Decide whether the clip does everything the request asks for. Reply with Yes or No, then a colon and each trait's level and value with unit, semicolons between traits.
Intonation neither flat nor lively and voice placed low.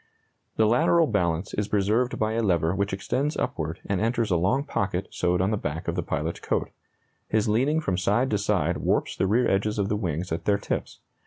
Yes: average, 3.6 semitones; low, 100 Hz